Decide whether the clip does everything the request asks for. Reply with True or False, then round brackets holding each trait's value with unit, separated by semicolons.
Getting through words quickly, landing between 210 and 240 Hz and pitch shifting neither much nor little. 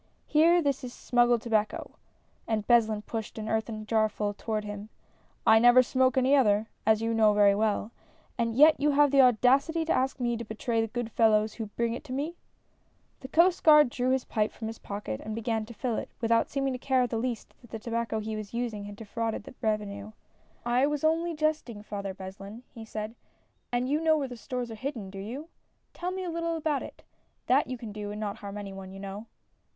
True (225 wpm; 230 Hz; 3.6 semitones)